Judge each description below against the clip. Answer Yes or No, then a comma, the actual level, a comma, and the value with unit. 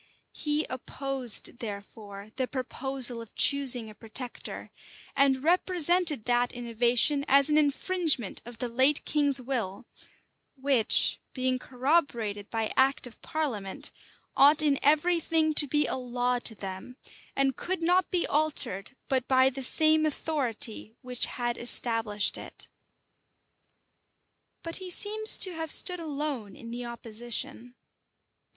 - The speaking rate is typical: No, slow, 130 wpm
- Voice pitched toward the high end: Yes, very high, 260 Hz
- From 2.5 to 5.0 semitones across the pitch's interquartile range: Yes, average, 4.1 semitones